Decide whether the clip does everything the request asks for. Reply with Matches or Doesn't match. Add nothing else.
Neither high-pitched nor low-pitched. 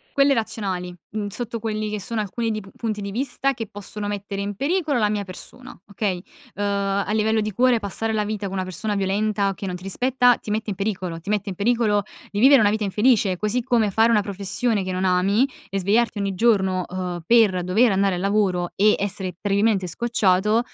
Doesn't match